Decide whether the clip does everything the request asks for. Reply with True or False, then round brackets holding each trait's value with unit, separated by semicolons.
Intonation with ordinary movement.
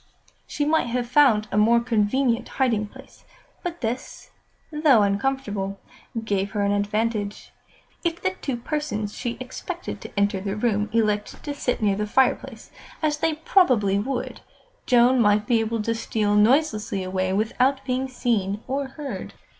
True (4.3 semitones)